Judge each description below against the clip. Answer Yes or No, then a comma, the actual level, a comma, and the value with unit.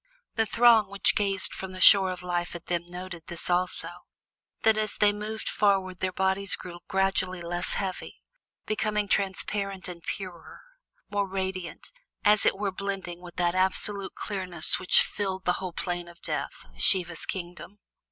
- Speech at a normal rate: Yes, average, 160 wpm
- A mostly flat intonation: Yes, narrow, 2.0 semitones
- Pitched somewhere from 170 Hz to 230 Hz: Yes, high, 190 Hz